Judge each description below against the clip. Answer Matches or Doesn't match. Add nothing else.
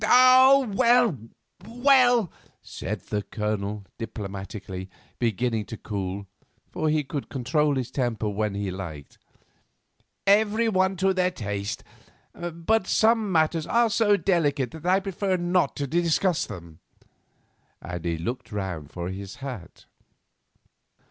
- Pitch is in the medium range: Matches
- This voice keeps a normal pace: Doesn't match